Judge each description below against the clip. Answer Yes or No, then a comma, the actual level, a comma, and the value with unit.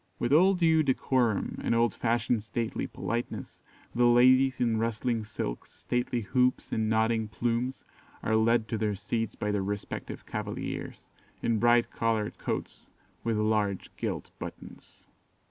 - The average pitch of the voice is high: No, low, 115 Hz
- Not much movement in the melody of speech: Yes, narrow, 2.1 semitones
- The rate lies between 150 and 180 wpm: No, average, 140 wpm